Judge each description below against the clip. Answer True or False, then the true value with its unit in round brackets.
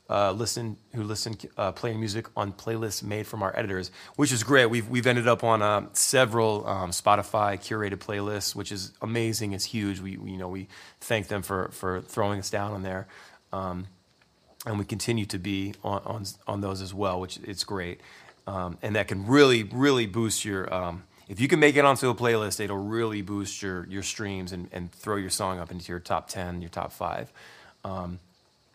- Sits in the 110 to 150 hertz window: False (100 Hz)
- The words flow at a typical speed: False (215 wpm)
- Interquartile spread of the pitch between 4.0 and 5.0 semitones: False (3.1 semitones)